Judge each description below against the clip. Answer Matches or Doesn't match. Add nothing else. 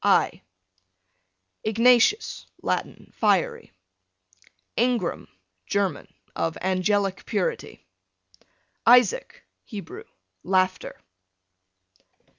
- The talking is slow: Matches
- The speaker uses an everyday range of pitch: Matches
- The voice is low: Doesn't match